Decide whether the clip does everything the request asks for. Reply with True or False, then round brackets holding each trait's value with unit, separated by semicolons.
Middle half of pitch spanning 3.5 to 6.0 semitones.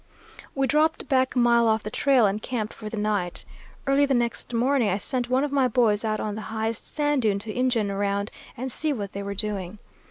True (3.8 semitones)